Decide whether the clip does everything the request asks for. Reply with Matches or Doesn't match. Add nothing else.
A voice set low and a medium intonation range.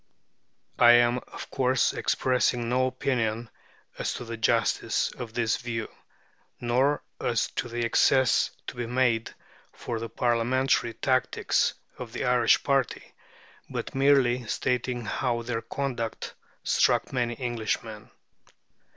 Doesn't match